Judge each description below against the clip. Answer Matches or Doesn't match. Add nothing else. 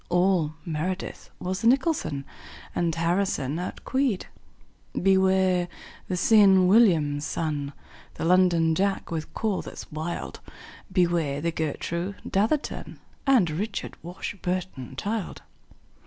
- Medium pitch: Matches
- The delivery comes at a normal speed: Doesn't match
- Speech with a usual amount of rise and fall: Matches